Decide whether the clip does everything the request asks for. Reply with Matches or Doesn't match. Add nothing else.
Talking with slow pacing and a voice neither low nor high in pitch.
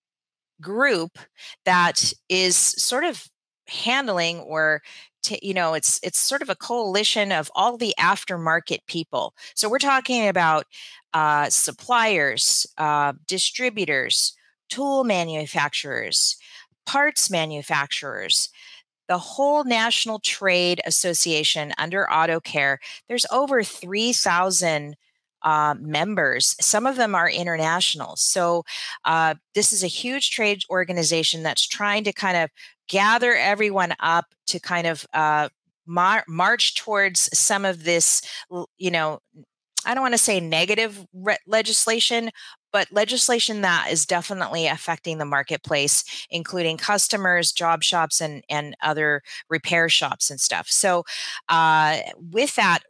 Matches